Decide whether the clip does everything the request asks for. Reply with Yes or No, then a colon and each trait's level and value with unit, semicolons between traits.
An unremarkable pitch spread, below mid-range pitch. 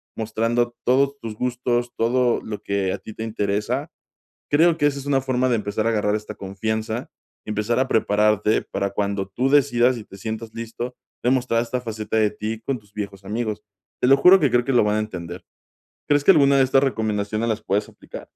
Yes: average, 3.1 semitones; low, 115 Hz